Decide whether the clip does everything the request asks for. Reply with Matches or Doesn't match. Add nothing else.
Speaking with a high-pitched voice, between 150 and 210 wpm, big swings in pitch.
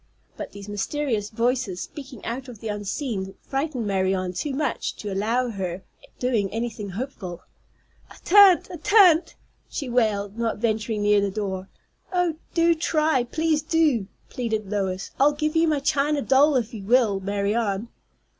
Matches